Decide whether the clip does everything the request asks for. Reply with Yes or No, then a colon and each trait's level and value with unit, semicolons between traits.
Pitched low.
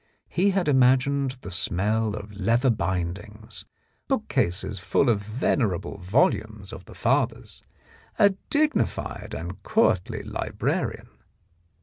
Yes: low, 110 Hz